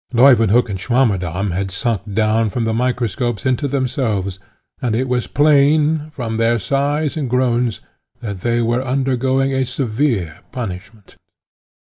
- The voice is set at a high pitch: No, low, 120 Hz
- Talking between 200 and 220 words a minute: No, slow, 135 wpm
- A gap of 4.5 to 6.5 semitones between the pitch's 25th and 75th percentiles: No, average, 3.7 semitones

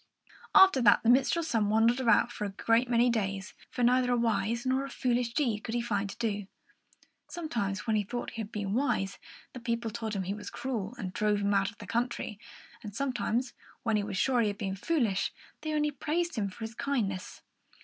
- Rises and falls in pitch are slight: No, average, 3.4 semitones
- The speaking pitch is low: No, high, 230 Hz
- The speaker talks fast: Yes, fast, 215 wpm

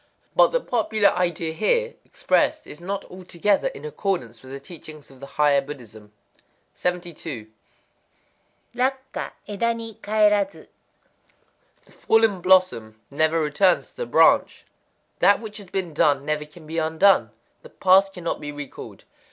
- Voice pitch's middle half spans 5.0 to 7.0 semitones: Yes, wide, 5.5 semitones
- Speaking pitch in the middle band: Yes, medium, 175 Hz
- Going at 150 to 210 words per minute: No, slow, 135 wpm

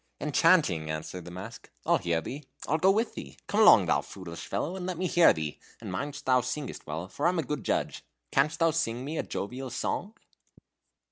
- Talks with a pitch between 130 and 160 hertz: Yes, low, 135 Hz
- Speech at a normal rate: No, fast, 210 wpm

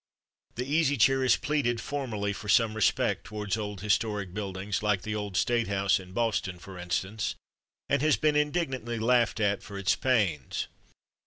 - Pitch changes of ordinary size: Yes, average, 4.0 semitones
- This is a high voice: No, low, 105 Hz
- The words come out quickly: No, average, 165 wpm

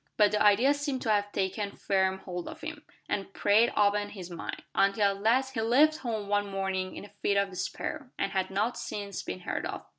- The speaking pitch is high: Yes, high, 205 Hz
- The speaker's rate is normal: No, fast, 215 wpm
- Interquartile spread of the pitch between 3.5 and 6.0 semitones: No, average, 3.0 semitones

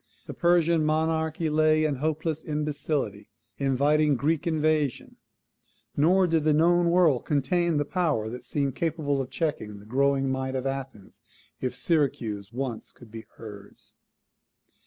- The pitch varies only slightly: No, average, 3.4 semitones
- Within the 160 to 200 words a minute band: No, slow, 135 wpm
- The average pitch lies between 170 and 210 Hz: No, medium, 150 Hz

